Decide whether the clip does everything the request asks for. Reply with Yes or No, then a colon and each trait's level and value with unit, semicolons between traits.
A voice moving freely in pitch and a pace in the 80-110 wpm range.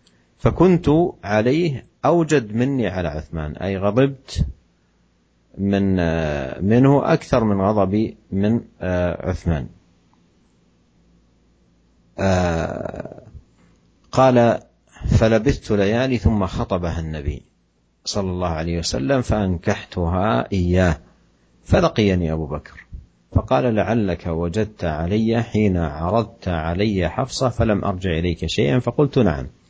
Yes: wide, 5.7 semitones; average, 90 wpm